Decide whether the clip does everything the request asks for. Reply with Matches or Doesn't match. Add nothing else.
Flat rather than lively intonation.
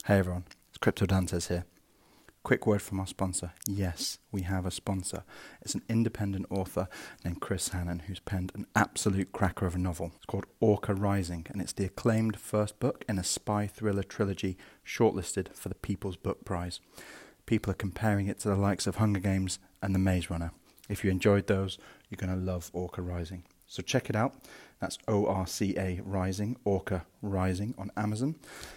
Matches